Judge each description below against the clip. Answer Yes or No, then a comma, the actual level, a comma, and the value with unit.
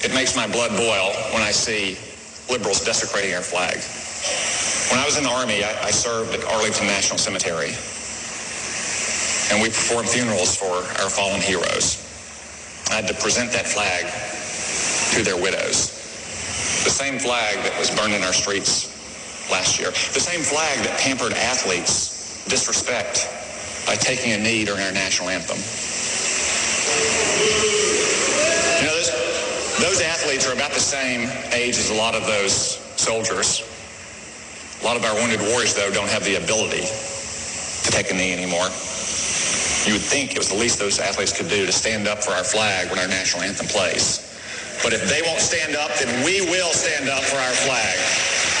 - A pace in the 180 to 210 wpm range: No, average, 165 wpm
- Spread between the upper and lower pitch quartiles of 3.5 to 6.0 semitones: Yes, average, 4.5 semitones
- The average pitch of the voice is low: Yes, low, 105 Hz